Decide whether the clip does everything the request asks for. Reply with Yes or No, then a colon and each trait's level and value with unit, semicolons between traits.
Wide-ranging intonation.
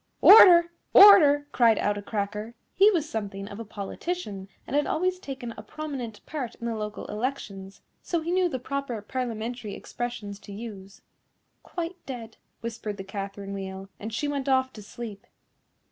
Yes: wide, 6.0 semitones